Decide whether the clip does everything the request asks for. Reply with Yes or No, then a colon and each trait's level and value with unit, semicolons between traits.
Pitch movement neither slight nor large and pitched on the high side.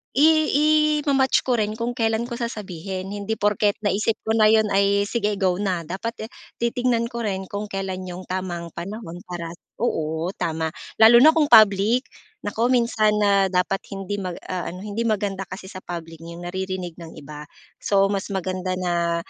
Yes: average, 3.6 semitones; high, 200 Hz